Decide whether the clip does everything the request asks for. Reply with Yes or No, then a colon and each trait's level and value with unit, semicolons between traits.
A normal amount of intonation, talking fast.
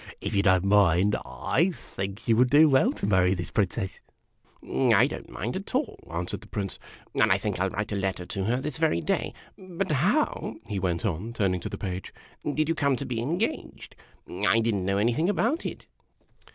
No: wide, 7.6 semitones; fast, 220 wpm